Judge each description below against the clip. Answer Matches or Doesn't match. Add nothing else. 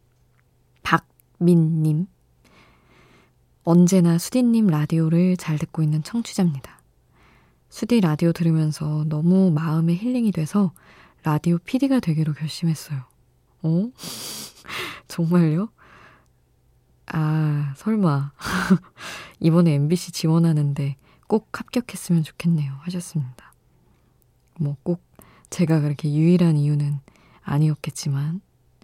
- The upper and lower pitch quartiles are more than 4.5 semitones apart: Doesn't match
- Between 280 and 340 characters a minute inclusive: Doesn't match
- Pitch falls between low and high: Matches